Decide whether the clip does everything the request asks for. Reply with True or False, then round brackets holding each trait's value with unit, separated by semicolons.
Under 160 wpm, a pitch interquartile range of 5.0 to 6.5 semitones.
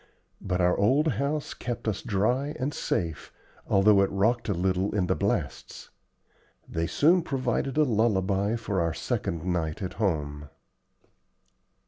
True (140 wpm; 5.3 semitones)